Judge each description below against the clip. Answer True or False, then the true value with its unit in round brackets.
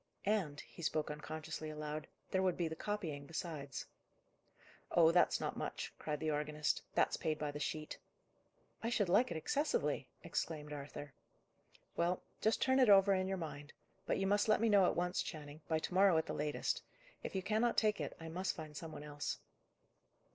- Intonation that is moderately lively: True (4.2 semitones)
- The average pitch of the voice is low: False (160 Hz)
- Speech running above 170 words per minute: True (190 wpm)